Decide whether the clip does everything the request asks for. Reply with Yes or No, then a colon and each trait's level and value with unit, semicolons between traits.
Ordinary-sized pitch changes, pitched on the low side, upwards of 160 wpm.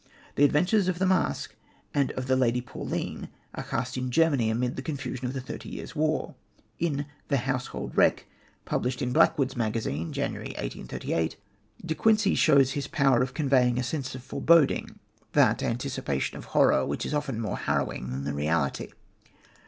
Yes: average, 3.5 semitones; low, 130 Hz; average, 170 wpm